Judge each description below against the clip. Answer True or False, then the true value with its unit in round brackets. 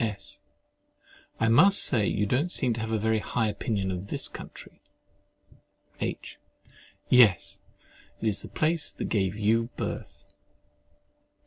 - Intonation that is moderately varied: True (3.1 semitones)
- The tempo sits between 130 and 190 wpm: True (135 wpm)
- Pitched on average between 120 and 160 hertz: False (110 Hz)